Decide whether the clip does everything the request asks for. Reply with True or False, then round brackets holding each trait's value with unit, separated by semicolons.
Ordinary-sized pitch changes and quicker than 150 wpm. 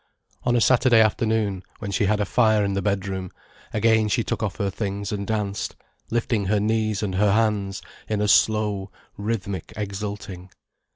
False (1.8 semitones; 170 wpm)